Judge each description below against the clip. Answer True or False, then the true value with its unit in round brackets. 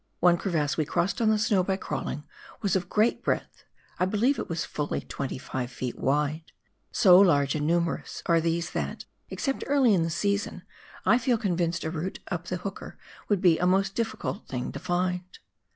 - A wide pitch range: False (3.6 semitones)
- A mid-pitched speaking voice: True (180 Hz)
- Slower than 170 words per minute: False (190 wpm)